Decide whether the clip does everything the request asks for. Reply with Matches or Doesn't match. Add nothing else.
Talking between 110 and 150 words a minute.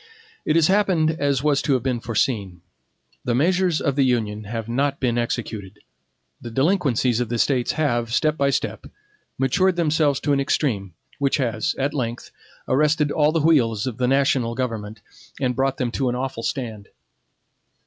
Doesn't match